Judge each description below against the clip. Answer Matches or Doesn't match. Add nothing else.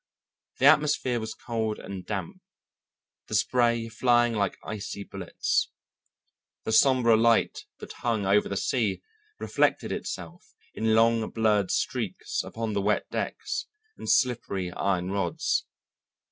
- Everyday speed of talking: Doesn't match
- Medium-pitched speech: Doesn't match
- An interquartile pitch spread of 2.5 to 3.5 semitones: Matches